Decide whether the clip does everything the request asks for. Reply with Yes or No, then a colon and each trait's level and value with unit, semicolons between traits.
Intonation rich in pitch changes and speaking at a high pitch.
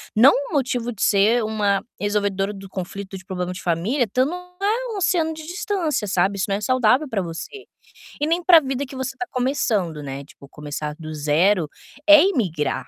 Yes: wide, 7.3 semitones; high, 215 Hz